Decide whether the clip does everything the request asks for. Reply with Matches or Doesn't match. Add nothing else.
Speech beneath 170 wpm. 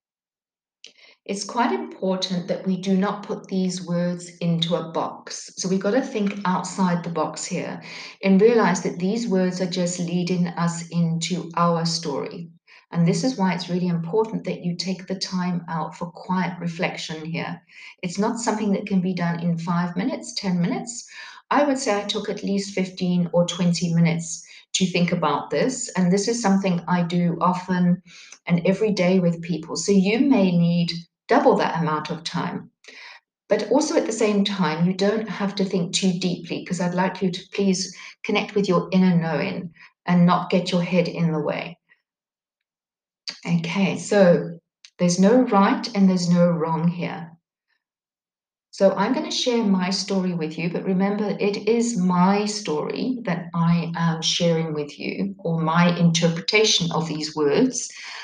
Doesn't match